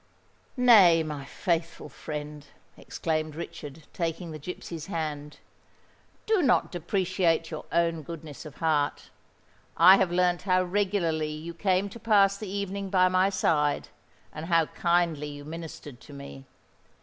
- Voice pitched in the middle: Yes, medium, 165 Hz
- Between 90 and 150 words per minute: Yes, slow, 135 wpm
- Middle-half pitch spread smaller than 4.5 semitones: Yes, average, 3.4 semitones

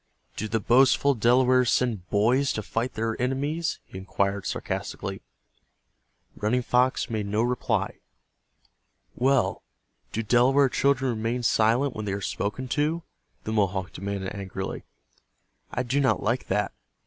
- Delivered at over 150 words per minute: No, slow, 135 wpm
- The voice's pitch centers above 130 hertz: No, low, 120 Hz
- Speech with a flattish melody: No, average, 3.9 semitones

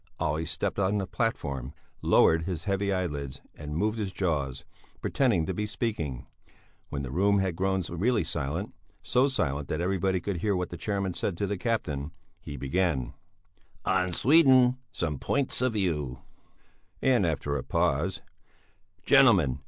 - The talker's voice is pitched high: No, very low, 90 Hz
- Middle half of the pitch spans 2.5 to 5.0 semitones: No, wide, 5.5 semitones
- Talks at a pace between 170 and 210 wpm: No, average, 150 wpm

